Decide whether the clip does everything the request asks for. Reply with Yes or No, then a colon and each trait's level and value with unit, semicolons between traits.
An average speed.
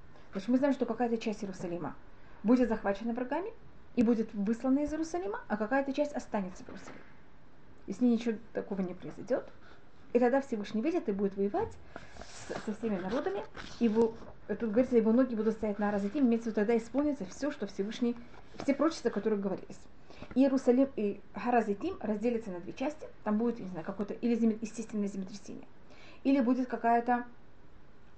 No: fast, 165 wpm